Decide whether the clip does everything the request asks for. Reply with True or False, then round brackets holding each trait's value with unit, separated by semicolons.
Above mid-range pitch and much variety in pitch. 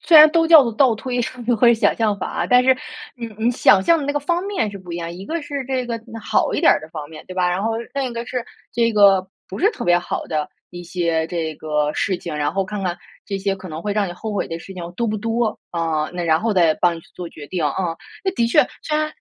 True (200 Hz; 5.9 semitones)